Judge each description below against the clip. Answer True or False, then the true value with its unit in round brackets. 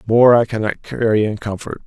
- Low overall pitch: True (110 Hz)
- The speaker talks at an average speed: True (195 wpm)